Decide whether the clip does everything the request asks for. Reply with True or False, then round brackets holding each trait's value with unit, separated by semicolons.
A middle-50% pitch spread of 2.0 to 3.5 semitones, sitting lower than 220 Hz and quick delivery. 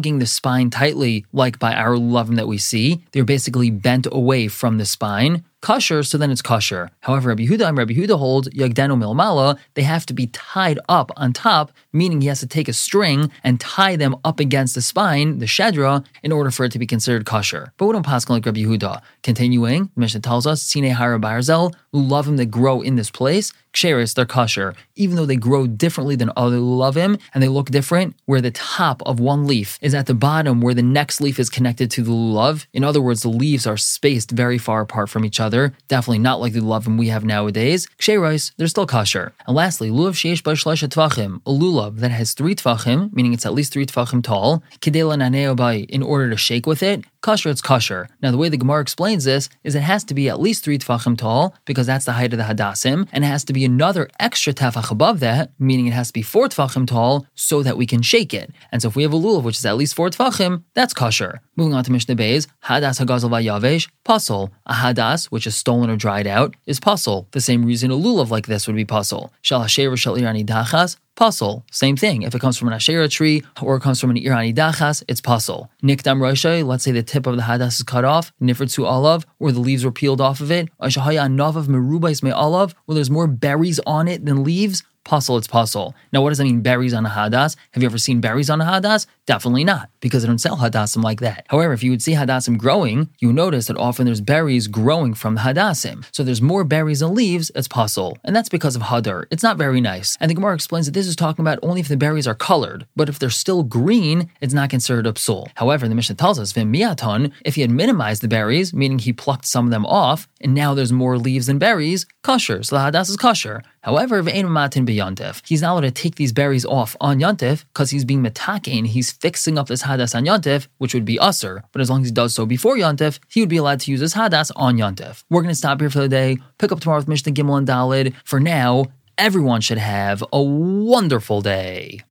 False (4.3 semitones; 135 Hz; 230 wpm)